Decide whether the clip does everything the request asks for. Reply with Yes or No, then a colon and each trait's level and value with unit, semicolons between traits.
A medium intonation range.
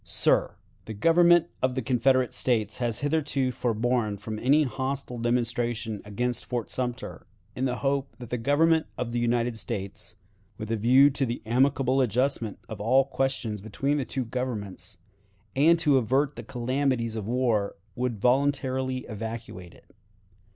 Yes: average, 3.0 semitones